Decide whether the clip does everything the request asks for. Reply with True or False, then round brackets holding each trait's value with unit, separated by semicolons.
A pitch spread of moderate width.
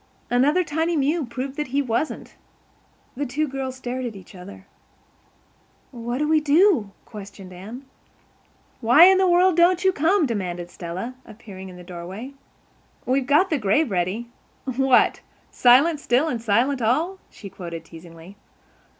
False (7.0 semitones)